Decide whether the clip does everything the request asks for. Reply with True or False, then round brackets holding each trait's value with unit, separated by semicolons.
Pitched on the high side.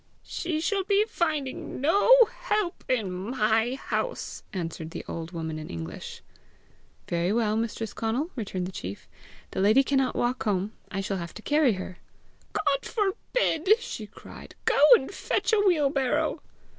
True (240 Hz)